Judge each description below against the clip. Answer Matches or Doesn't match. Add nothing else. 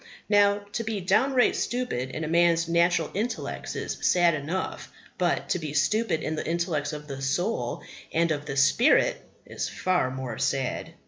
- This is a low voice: Doesn't match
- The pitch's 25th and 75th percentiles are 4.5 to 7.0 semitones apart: Matches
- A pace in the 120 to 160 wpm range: Doesn't match